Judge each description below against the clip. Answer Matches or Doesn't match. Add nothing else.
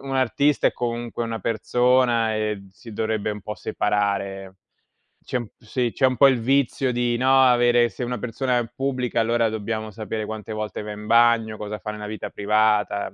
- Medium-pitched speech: Doesn't match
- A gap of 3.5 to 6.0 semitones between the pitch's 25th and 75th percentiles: Doesn't match